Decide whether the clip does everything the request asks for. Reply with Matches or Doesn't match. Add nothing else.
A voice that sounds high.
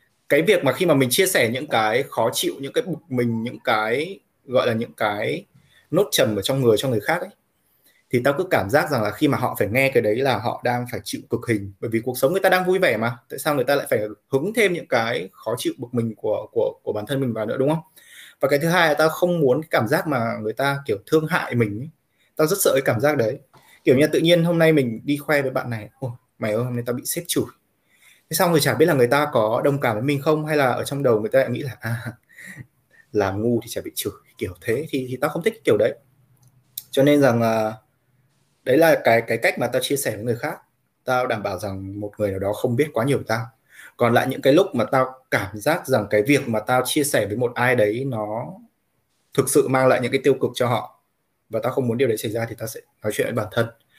Doesn't match